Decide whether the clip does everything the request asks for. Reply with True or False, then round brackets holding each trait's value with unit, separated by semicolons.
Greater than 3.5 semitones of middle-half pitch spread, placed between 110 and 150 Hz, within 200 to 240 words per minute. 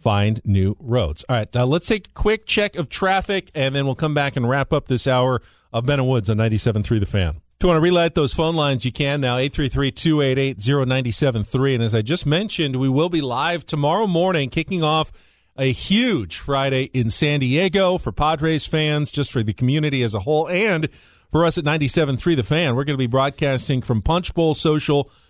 True (4.2 semitones; 140 Hz; 205 wpm)